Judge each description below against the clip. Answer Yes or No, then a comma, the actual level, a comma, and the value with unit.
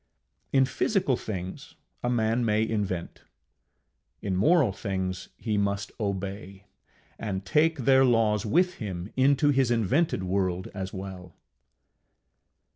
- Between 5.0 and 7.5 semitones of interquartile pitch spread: Yes, average, 5.3 semitones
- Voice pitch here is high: No, low, 105 Hz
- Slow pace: Yes, slow, 120 wpm